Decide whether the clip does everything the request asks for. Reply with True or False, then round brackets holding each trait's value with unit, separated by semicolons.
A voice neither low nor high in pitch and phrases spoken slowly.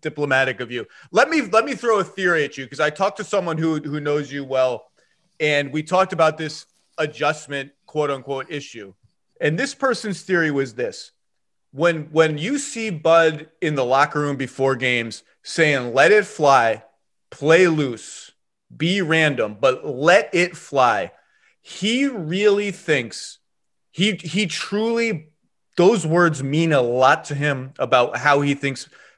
False (155 Hz; 160 wpm)